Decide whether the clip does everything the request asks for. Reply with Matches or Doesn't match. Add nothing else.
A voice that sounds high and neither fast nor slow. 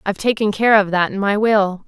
Doesn't match